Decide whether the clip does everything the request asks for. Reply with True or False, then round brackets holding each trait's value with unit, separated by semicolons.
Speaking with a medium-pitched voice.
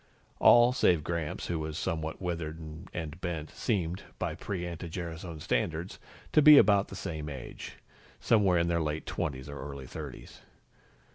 False (85 Hz)